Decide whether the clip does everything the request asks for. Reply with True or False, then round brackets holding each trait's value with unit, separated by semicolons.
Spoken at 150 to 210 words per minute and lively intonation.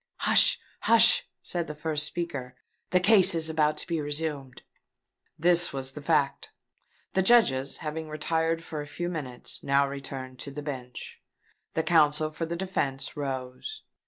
False (160 wpm; 3.4 semitones)